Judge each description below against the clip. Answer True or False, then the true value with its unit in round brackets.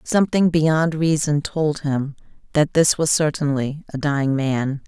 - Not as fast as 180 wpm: True (150 wpm)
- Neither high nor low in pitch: True (150 Hz)